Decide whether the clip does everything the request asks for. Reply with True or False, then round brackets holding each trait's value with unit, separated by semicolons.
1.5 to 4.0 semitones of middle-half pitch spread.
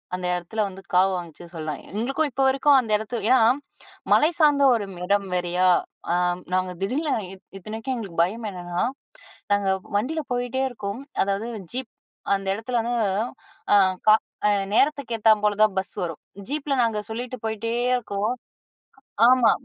False (4.6 semitones)